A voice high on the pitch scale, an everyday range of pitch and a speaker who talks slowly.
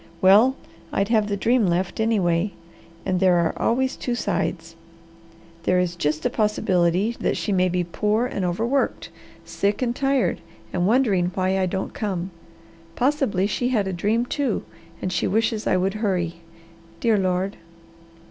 No: high, 195 Hz; average, 4.0 semitones; average, 155 wpm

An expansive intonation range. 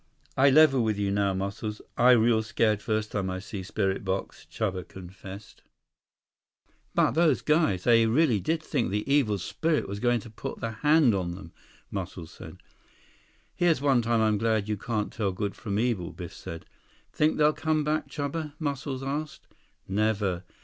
Yes: wide, 5.9 semitones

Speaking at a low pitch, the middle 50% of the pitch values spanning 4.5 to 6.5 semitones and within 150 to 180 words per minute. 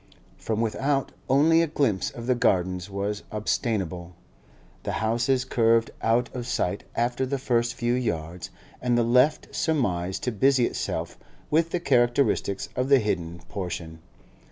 No: low, 120 Hz; average, 5.0 semitones; average, 140 wpm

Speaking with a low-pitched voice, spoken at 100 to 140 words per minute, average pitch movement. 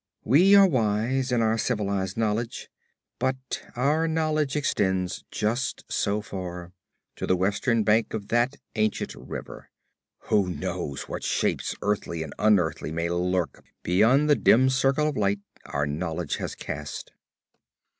No: low, 110 Hz; slow, 135 wpm; wide, 6.0 semitones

